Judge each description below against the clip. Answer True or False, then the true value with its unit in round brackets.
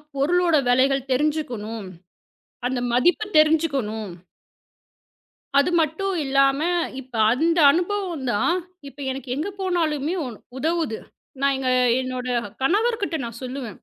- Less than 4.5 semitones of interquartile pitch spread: False (4.8 semitones)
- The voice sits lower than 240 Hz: False (280 Hz)